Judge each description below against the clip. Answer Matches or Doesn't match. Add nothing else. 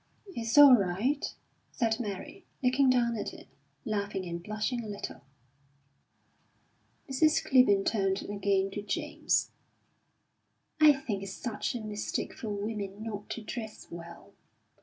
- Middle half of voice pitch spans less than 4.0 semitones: Matches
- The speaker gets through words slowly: Matches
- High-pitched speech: Matches